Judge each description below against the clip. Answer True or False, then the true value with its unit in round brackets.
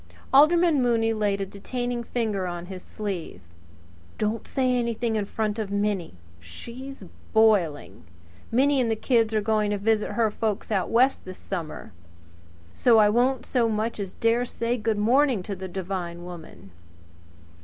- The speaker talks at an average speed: True (160 wpm)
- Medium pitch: False (215 Hz)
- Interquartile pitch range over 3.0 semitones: True (3.4 semitones)